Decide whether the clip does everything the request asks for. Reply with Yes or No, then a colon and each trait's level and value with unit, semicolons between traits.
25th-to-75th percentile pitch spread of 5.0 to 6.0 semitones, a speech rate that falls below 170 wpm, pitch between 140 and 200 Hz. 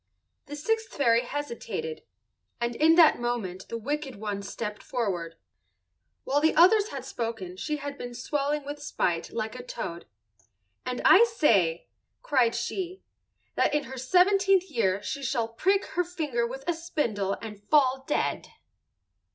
No: average, 5.3 semitones; average, 150 wpm; very high, 260 Hz